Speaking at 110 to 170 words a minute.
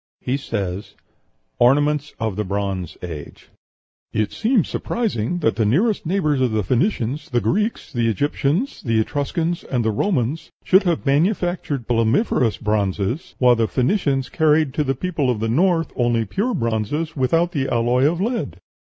Yes: average, 155 wpm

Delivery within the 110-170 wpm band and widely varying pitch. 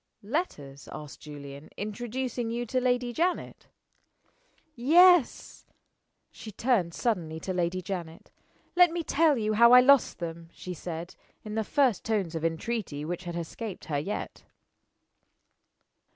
Yes: slow, 135 wpm; wide, 6.9 semitones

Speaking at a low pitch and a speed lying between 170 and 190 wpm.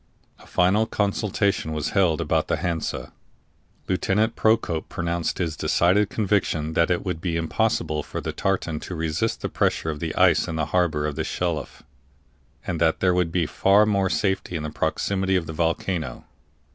Yes: very low, 85 Hz; average, 175 wpm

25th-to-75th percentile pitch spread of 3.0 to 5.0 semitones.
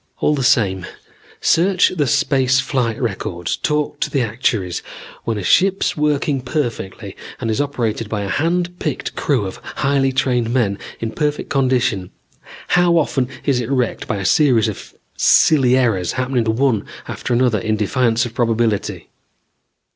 Yes: average, 4.3 semitones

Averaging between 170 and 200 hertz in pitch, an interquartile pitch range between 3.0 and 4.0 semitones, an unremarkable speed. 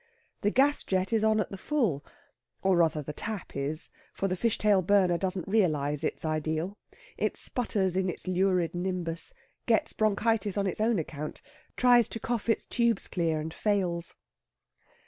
No: high, 190 Hz; average, 4.5 semitones; average, 165 wpm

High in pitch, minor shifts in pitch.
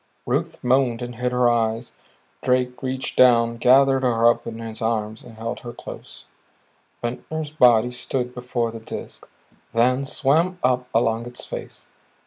No: low, 125 Hz; narrow, 1.7 semitones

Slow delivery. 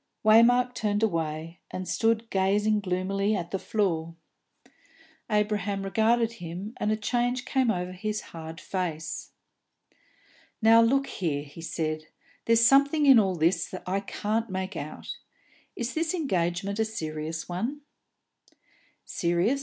Yes: slow, 130 wpm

